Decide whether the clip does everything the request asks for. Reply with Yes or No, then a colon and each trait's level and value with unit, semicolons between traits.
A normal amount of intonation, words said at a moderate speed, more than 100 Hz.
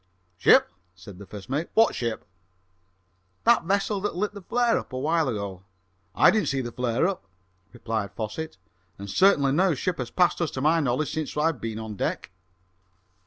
No: wide, 8.1 semitones; average, 180 wpm; medium, 140 Hz